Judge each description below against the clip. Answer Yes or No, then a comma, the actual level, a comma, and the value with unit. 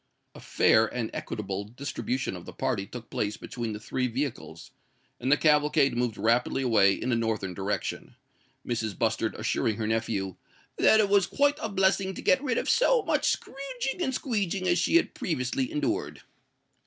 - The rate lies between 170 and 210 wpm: Yes, average, 175 wpm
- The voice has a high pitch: No, low, 125 Hz